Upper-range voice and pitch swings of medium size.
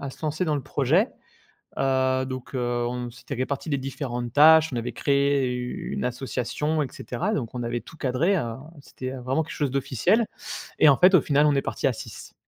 No: low, 135 Hz; average, 3.2 semitones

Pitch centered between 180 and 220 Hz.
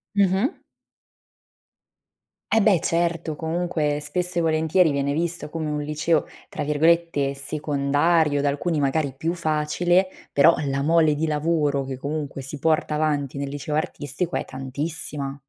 No: medium, 155 Hz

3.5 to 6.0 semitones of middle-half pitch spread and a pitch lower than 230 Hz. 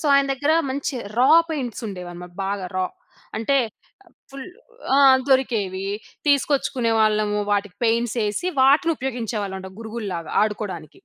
Yes: average, 5.2 semitones; high, 220 Hz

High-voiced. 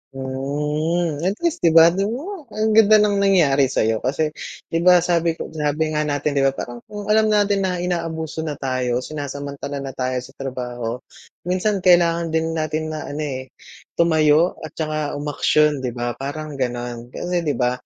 No: medium, 155 Hz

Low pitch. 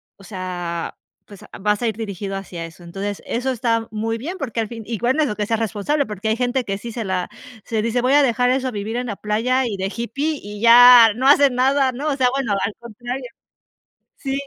No: high, 230 Hz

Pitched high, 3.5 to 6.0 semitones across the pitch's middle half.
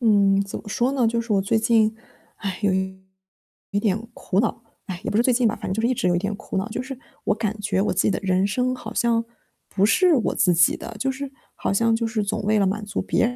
No: high, 215 Hz; average, 2.8 semitones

